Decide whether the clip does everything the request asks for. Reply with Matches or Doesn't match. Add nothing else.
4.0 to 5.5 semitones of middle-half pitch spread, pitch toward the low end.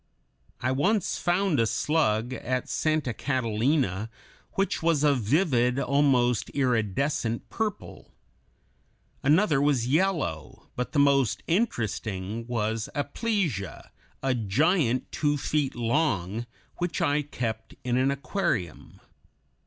Matches